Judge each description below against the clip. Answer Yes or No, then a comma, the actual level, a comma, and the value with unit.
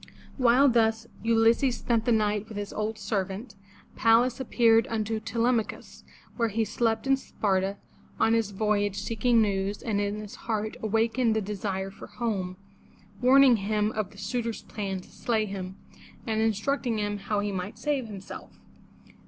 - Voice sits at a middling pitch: No, high, 220 Hz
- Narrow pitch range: Yes, narrow, 2.2 semitones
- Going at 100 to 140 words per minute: No, average, 160 wpm